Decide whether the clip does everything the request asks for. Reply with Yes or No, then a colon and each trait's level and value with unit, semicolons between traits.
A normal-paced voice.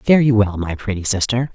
No: fast, 230 wpm